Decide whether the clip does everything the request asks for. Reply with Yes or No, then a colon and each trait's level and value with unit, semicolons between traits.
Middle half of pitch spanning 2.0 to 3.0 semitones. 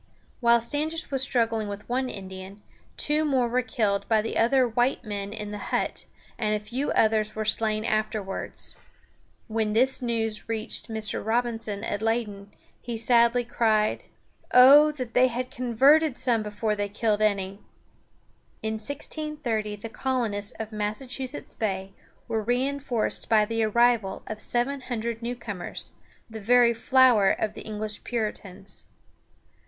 Yes: average, 2.7 semitones